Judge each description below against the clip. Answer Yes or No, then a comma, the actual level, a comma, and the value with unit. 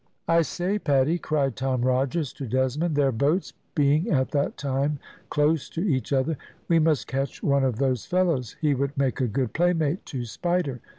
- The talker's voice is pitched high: No, medium, 140 Hz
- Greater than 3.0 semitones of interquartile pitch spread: Yes, average, 3.6 semitones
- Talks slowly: No, average, 180 wpm